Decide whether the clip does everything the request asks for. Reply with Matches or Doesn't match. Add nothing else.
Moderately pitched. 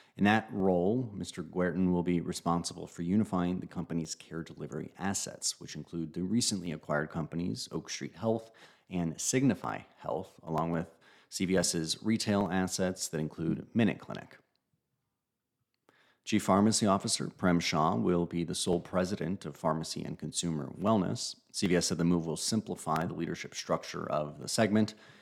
Doesn't match